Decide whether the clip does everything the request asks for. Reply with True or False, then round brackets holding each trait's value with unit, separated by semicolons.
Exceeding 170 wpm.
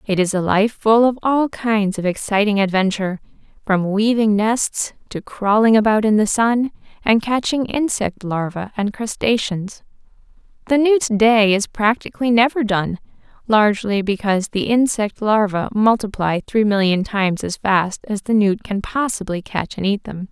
False (155 wpm)